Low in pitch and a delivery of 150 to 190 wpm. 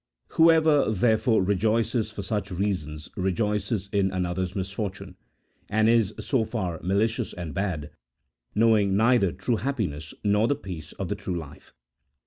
No: low, 100 Hz; slow, 135 wpm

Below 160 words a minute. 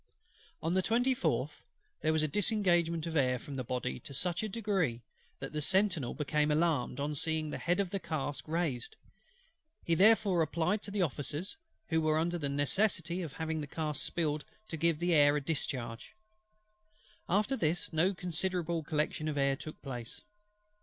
No: average, 175 wpm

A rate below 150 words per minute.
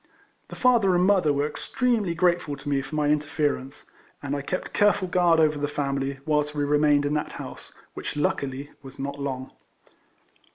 No: average, 175 wpm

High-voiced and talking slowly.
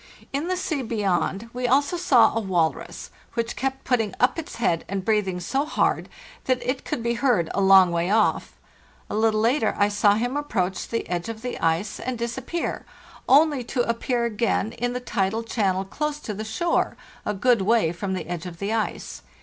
No: high, 225 Hz; average, 195 wpm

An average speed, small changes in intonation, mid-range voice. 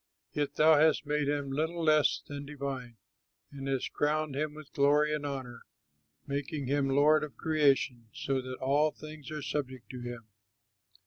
Yes: average, 165 wpm; narrow, 2.1 semitones; medium, 145 Hz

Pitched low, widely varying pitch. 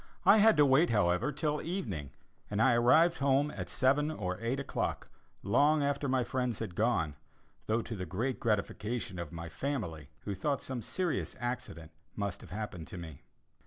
Yes: low, 120 Hz; wide, 7.3 semitones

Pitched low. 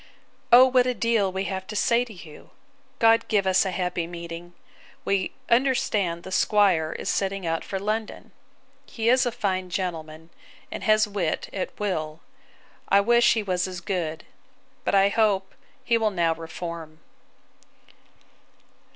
No: high, 190 Hz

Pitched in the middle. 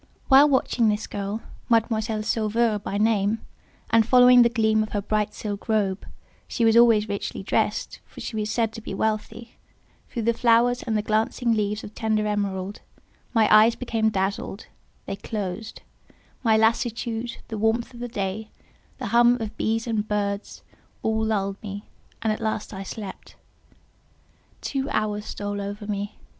No: high, 220 Hz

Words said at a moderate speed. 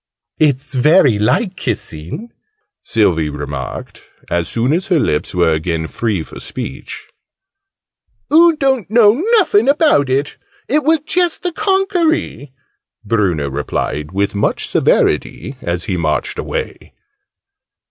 No: slow, 120 wpm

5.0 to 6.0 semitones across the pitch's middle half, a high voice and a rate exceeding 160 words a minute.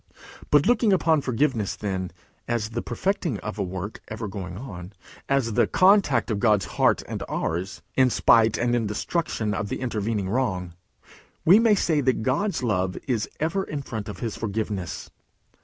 No: average, 5.3 semitones; low, 115 Hz; average, 170 wpm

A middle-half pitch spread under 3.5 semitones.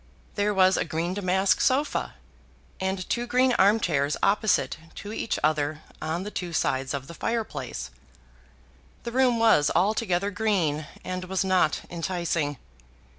No: average, 5.0 semitones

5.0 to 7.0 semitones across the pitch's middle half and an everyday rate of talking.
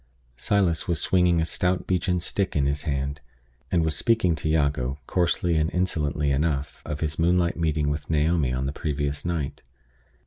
No: average, 3.2 semitones; average, 170 wpm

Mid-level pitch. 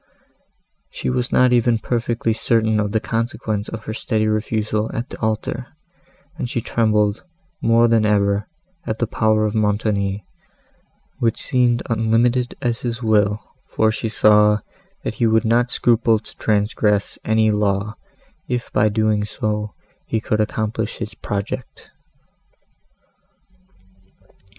No: low, 110 Hz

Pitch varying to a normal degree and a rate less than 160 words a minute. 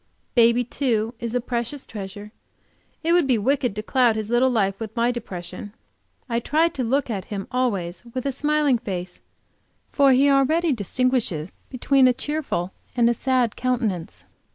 No: average, 4.0 semitones; average, 165 wpm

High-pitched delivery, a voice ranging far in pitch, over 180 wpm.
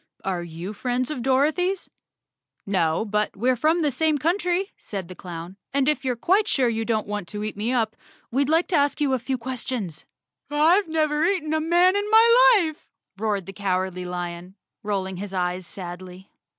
Yes: high, 240 Hz; wide, 8.6 semitones; average, 190 wpm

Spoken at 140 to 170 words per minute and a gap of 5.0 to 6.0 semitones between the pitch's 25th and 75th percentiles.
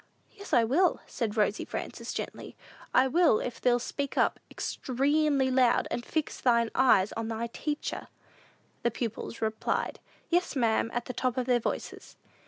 No: average, 160 wpm; average, 3.5 semitones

